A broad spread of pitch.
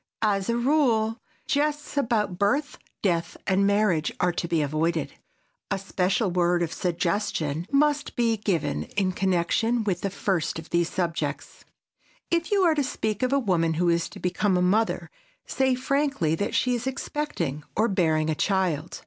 Yes: wide, 6.0 semitones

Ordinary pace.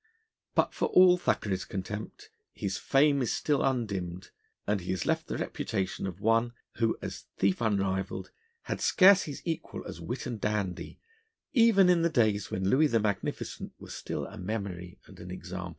Yes: average, 170 wpm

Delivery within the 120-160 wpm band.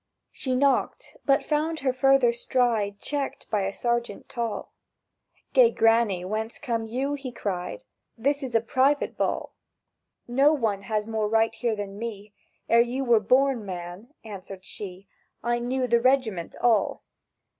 Yes: average, 150 wpm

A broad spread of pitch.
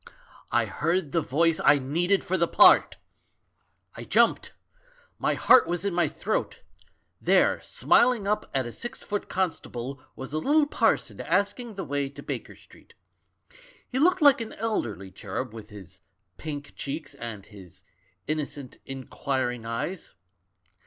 Yes: wide, 7.4 semitones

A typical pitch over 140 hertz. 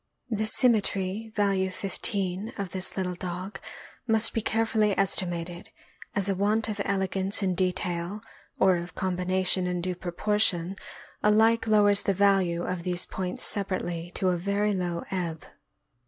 Yes: high, 190 Hz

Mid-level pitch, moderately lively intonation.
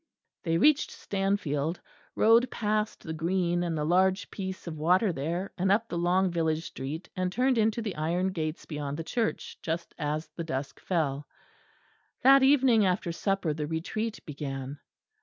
Yes: medium, 175 Hz; average, 4.3 semitones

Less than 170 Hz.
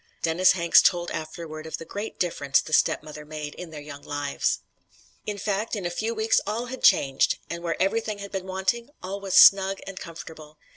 No: medium, 180 Hz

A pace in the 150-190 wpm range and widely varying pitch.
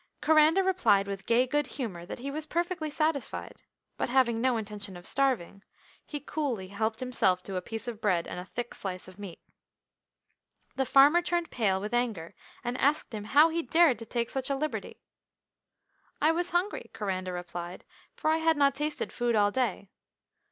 Yes: average, 180 wpm; wide, 7.0 semitones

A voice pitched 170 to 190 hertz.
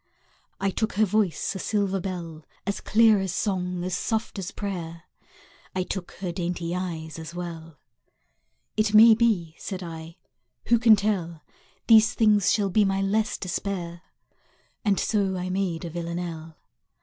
Yes: medium, 185 Hz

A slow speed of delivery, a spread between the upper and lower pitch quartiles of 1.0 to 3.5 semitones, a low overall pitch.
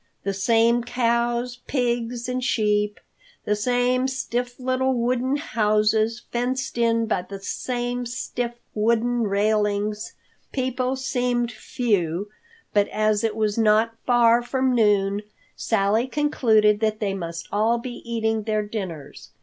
No: slow, 125 wpm; narrow, 2.6 semitones; high, 230 Hz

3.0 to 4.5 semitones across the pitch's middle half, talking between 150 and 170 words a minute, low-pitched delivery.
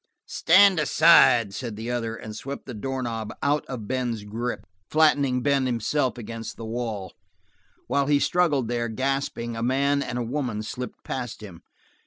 Yes: average, 3.6 semitones; average, 160 wpm; low, 125 Hz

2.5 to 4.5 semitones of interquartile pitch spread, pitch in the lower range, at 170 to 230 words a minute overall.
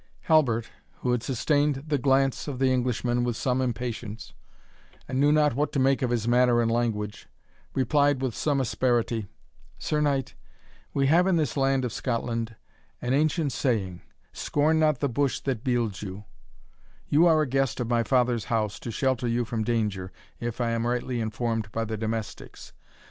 Yes: average, 3.1 semitones; low, 125 Hz; average, 175 wpm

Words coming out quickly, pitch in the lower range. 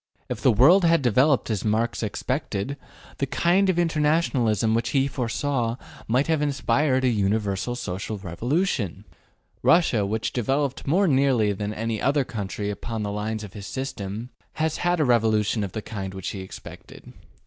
No: average, 165 wpm; low, 120 Hz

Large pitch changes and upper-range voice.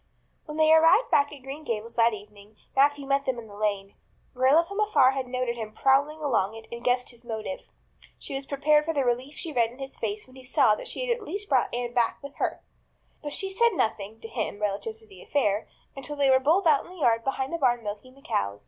No: average, 4.6 semitones; very high, 260 Hz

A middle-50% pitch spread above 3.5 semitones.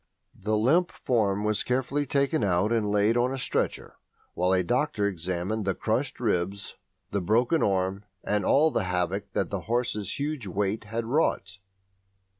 Yes: average, 4.3 semitones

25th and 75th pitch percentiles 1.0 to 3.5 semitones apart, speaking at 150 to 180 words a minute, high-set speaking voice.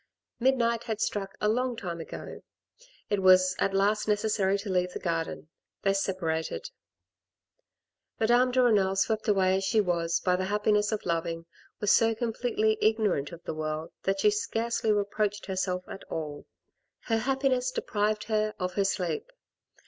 Yes: average, 3.2 semitones; average, 160 wpm; high, 205 Hz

